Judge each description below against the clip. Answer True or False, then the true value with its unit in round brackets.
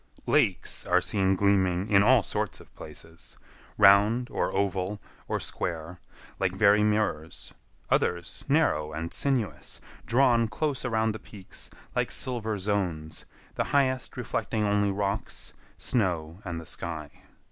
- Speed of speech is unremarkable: False (125 wpm)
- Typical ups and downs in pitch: True (4.0 semitones)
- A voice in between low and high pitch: False (100 Hz)